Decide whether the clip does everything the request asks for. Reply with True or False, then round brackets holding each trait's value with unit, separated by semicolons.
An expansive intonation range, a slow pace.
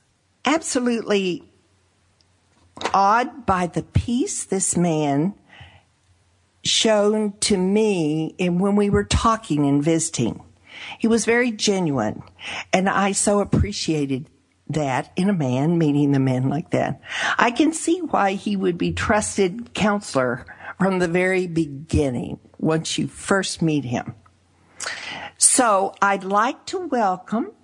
True (7.1 semitones; 125 wpm)